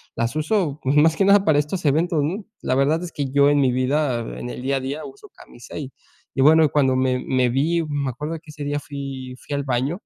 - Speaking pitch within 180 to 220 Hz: No, medium, 145 Hz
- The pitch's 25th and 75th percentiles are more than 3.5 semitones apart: No, average, 3.2 semitones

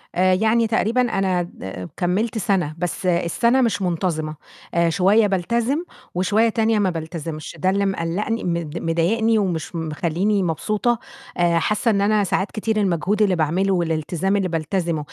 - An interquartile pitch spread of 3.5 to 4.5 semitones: Yes, average, 4.1 semitones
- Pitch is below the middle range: No, medium, 185 Hz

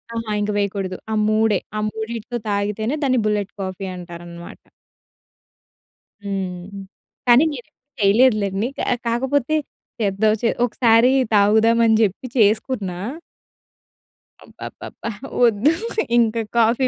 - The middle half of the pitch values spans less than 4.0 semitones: Yes, average, 2.8 semitones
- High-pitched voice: Yes, high, 215 Hz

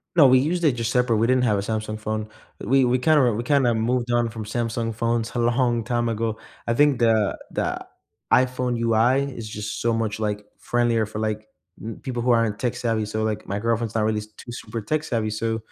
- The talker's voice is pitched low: Yes, low, 115 Hz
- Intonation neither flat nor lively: No, narrow, 2.1 semitones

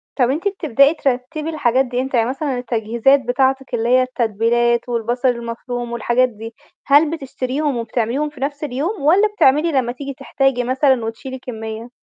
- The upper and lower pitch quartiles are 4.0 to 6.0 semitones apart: No, average, 2.8 semitones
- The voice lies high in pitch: Yes, very high, 255 Hz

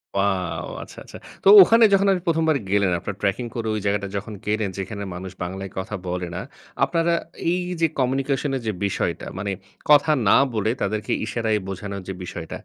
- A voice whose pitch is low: Yes, low, 105 Hz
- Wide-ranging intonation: Yes, wide, 5.7 semitones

